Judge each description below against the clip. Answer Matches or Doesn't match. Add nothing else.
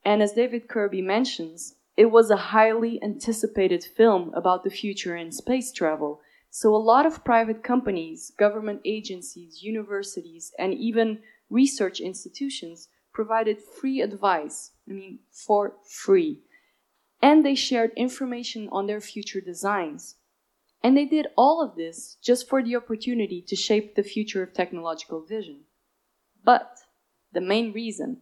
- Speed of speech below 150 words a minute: Matches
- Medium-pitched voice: Doesn't match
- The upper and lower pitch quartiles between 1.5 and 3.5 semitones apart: Doesn't match